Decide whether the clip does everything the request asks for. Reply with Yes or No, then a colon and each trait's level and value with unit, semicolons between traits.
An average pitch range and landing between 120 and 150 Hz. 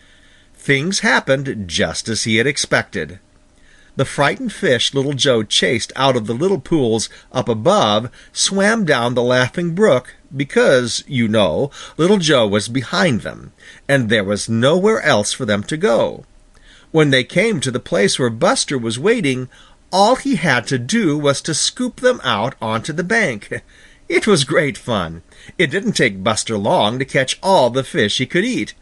No: wide, 6.6 semitones; low, 135 Hz